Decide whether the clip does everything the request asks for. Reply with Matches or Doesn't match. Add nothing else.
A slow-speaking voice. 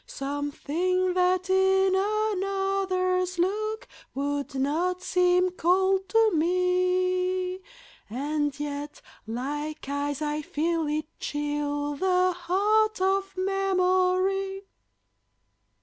Matches